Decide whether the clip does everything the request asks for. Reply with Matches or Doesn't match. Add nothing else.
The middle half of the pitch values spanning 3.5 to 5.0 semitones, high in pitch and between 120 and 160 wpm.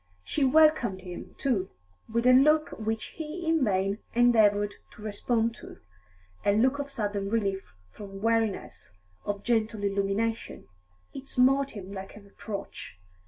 Matches